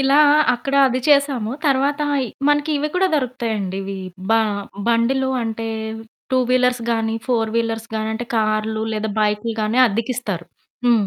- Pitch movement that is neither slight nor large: Yes, average, 3.2 semitones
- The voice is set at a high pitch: Yes, high, 230 Hz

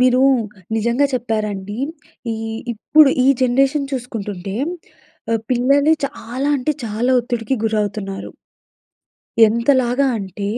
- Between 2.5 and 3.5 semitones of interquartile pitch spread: No, average, 3.9 semitones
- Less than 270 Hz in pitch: Yes, high, 240 Hz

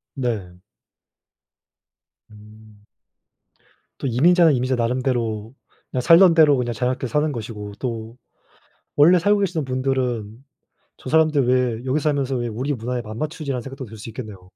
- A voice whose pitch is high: No, low, 125 Hz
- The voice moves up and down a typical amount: Yes, average, 4.2 semitones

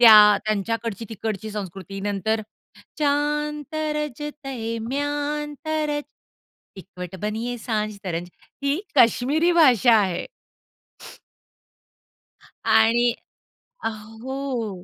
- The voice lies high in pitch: Yes, high, 235 Hz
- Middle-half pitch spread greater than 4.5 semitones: Yes, wide, 5.5 semitones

